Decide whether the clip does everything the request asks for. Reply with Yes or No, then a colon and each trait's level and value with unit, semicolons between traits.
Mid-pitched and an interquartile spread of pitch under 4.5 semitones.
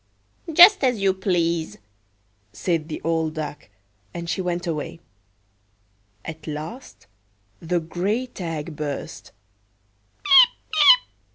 Yes: medium, 165 Hz; average, 3.4 semitones